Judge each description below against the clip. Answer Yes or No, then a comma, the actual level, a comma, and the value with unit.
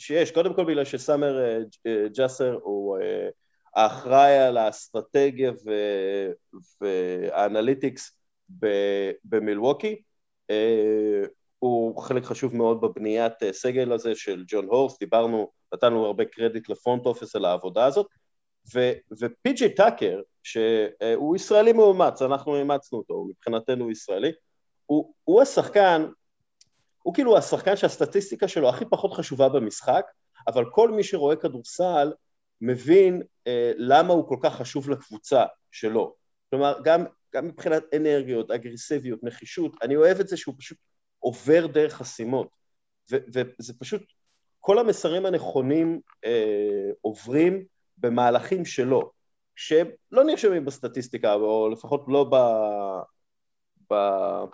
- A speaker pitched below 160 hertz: Yes, medium, 140 Hz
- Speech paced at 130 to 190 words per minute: No, average, 120 wpm